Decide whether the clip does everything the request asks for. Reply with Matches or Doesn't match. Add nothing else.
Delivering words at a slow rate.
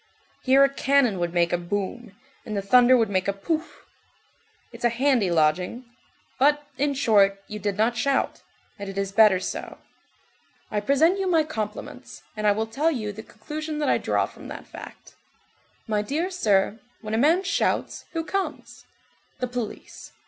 Doesn't match